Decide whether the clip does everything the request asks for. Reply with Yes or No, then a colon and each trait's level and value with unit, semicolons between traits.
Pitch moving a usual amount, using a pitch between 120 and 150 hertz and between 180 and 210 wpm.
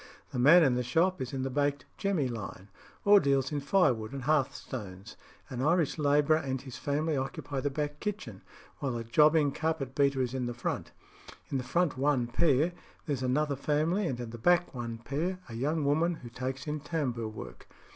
Yes: average, 3.7 semitones; medium, 140 Hz; average, 195 wpm